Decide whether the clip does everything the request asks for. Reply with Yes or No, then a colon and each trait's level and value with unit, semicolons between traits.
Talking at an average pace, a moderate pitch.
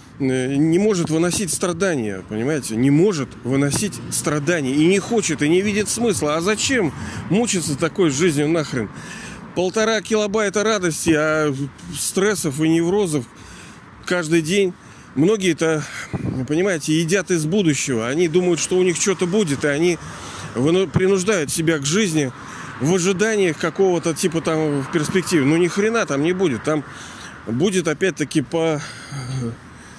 Yes: average, 135 wpm; medium, 165 Hz